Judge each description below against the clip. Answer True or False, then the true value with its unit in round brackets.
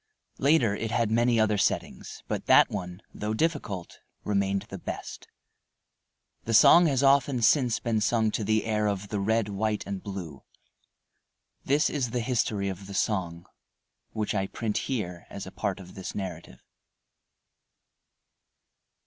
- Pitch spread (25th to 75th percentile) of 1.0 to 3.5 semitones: True (3.0 semitones)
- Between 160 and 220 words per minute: False (150 wpm)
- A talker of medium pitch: False (105 Hz)